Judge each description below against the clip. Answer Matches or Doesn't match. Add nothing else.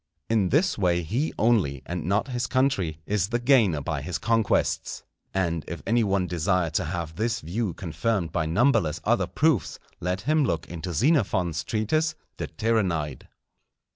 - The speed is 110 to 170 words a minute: Matches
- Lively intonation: Matches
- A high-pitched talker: Doesn't match